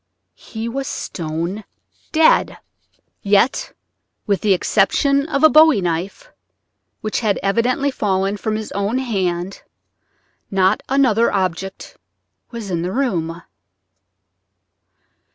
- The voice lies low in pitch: No, high, 205 Hz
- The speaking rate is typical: No, slow, 105 wpm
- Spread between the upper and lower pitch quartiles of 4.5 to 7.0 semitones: Yes, average, 5.1 semitones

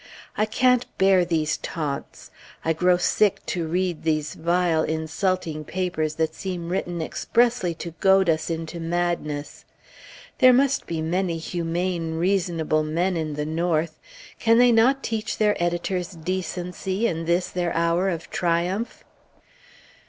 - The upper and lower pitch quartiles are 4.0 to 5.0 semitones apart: No, narrow, 2.6 semitones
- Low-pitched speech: No, medium, 175 Hz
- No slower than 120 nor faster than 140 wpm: Yes, slow, 135 wpm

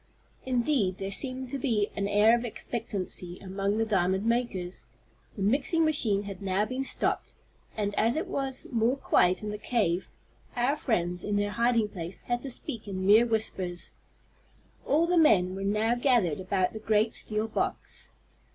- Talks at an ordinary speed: Yes, average, 170 wpm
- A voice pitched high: Yes, high, 215 Hz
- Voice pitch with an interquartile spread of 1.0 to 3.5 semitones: No, average, 3.9 semitones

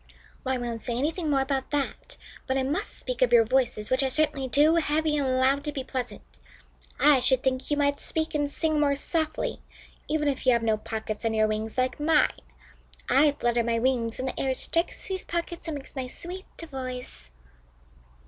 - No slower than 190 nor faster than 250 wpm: Yes, average, 200 wpm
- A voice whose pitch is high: Yes, very high, 270 Hz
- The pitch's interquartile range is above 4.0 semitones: No, average, 3.1 semitones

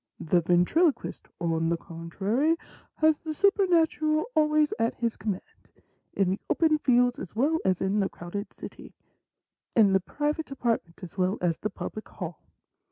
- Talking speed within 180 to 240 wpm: No, average, 160 wpm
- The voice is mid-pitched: No, high, 220 Hz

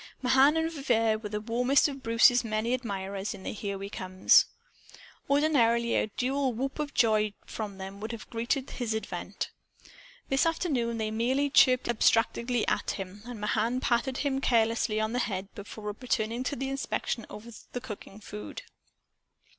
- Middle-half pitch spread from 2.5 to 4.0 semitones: Yes, average, 3.3 semitones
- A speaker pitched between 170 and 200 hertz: No, high, 230 Hz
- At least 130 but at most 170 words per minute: Yes, average, 160 wpm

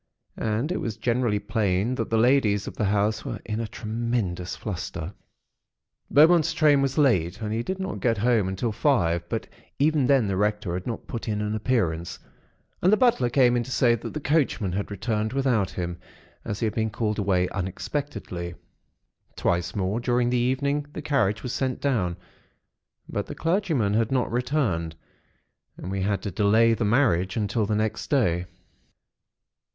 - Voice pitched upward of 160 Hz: No, low, 110 Hz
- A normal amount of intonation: Yes, average, 4.5 semitones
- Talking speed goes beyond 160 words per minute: Yes, average, 175 wpm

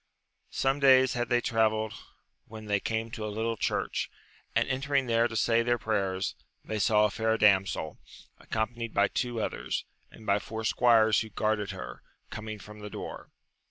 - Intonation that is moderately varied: No, narrow, 1.8 semitones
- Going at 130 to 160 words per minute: No, average, 170 wpm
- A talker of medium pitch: No, low, 110 Hz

